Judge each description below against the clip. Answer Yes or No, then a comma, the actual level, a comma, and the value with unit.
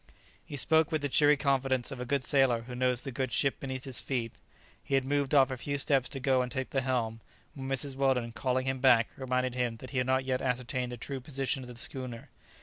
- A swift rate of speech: Yes, fast, 240 wpm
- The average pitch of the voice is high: No, low, 130 Hz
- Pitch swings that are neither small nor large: No, narrow, 1.5 semitones